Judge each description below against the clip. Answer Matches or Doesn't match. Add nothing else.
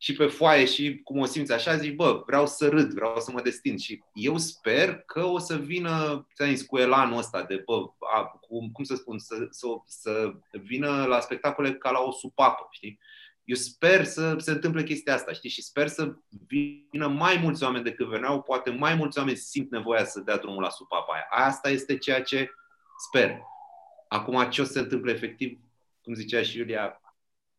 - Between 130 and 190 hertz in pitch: Matches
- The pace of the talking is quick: Matches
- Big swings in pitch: Doesn't match